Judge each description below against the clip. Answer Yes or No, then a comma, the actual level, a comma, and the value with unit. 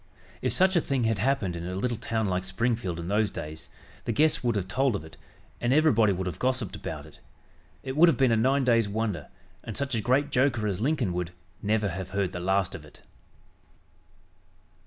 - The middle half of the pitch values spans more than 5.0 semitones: Yes, wide, 5.5 semitones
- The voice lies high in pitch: No, low, 110 Hz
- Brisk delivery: Yes, fast, 210 wpm